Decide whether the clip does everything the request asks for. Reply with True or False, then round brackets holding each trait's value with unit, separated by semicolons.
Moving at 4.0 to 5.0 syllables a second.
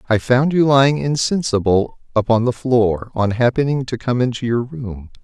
True (4.8 syllables/s)